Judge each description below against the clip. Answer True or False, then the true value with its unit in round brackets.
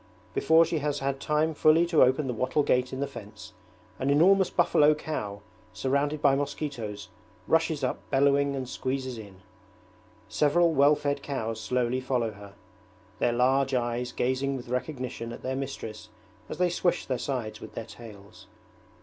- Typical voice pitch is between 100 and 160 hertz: True (135 Hz)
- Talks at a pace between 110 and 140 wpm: False (160 wpm)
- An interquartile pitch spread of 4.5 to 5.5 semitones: False (3.6 semitones)